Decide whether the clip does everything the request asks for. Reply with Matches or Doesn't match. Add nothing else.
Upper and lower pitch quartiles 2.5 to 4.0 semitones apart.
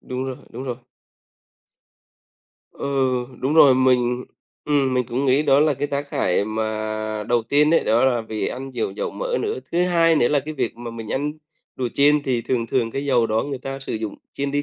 Matches